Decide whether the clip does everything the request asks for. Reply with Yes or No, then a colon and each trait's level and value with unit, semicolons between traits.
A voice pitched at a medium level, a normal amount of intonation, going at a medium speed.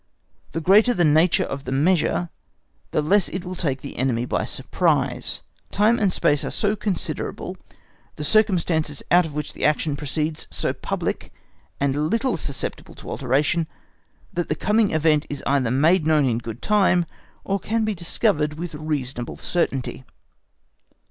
Yes: medium, 155 Hz; average, 4.6 semitones; average, 155 wpm